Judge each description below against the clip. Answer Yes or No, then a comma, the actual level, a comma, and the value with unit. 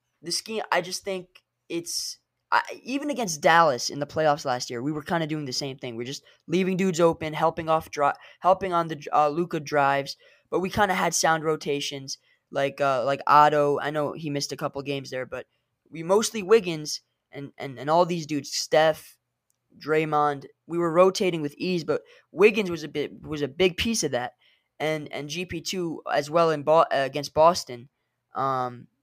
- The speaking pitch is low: No, medium, 155 Hz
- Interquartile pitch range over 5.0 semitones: No, average, 3.9 semitones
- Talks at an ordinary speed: Yes, average, 190 wpm